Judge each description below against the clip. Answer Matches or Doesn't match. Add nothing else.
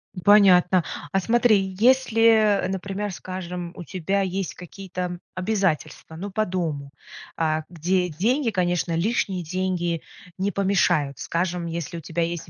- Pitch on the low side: Doesn't match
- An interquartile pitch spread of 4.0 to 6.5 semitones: Doesn't match